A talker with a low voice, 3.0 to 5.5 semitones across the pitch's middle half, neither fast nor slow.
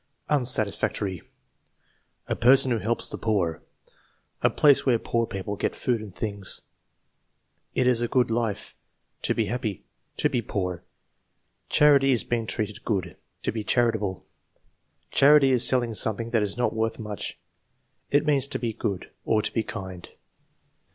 Yes: low, 115 Hz; average, 3.3 semitones; average, 160 wpm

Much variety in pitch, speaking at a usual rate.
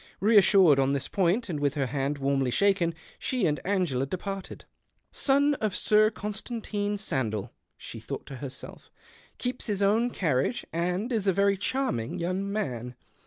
Yes: wide, 7.0 semitones; average, 165 wpm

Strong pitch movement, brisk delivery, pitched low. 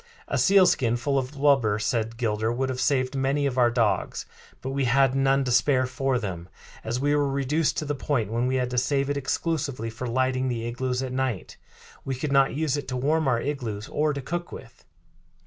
No: average, 2.7 semitones; fast, 215 wpm; low, 130 Hz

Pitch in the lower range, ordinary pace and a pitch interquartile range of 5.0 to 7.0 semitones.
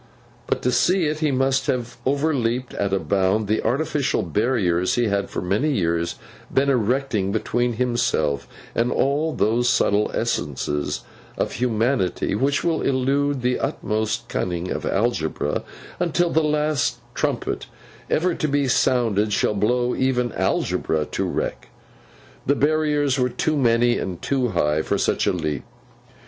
Yes: low, 120 Hz; average, 145 wpm; wide, 5.5 semitones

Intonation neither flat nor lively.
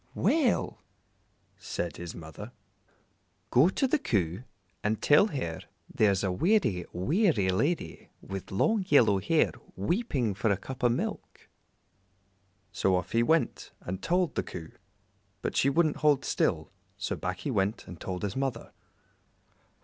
No: wide, 8.6 semitones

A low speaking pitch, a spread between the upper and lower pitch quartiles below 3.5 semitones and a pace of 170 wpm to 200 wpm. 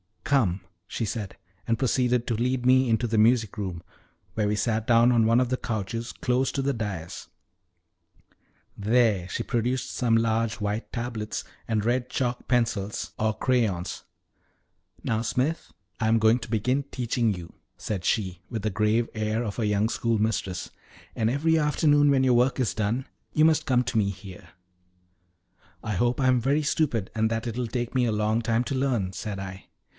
Yes: low, 115 Hz; average, 2.9 semitones; average, 180 wpm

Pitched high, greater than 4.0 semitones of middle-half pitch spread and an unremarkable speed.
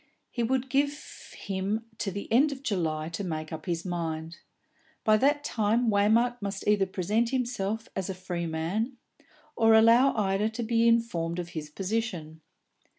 Yes: high, 205 Hz; average, 5.1 semitones; average, 160 wpm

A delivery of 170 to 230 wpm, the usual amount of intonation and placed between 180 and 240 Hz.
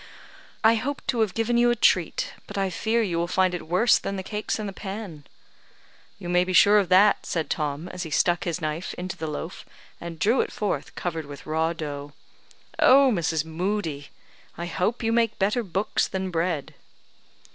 Yes: average, 195 wpm; average, 4.4 semitones; medium, 185 Hz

